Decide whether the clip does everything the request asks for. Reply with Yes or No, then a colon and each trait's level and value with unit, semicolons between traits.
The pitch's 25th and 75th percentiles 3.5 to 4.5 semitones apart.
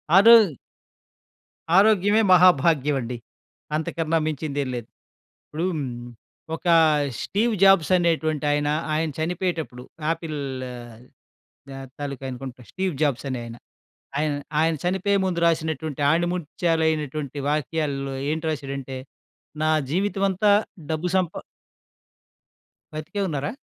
Yes: average, 3.8 semitones